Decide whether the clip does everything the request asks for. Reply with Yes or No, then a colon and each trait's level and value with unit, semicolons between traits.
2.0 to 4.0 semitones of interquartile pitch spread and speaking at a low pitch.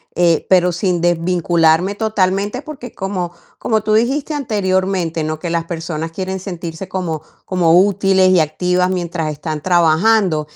No: average, 2.8 semitones; medium, 180 Hz